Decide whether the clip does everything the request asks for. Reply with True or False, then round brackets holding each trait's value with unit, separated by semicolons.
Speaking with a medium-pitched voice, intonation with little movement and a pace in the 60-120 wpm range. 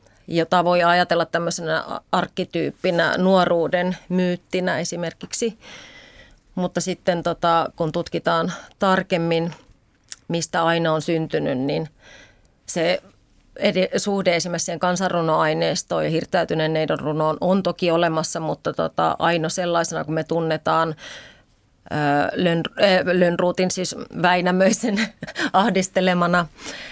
True (175 Hz; 1.8 semitones; 100 wpm)